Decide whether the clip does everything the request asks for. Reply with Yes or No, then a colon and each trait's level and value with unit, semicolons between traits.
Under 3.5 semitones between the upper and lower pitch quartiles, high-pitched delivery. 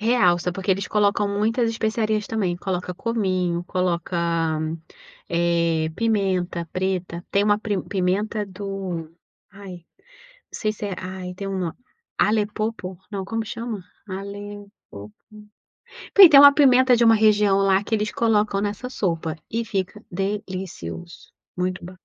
Yes: average, 2.9 semitones; high, 200 Hz